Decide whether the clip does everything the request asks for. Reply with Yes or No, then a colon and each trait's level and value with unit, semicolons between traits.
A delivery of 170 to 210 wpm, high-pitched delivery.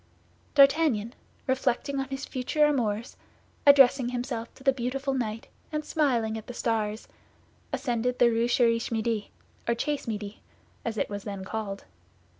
No: average, 145 wpm; high, 240 Hz